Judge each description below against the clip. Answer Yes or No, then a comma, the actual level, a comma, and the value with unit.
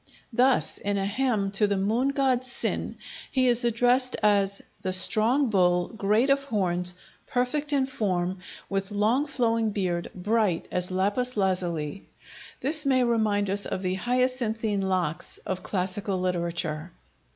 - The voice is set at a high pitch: Yes, high, 205 Hz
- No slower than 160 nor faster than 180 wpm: No, average, 140 wpm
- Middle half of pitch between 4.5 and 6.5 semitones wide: Yes, average, 5.0 semitones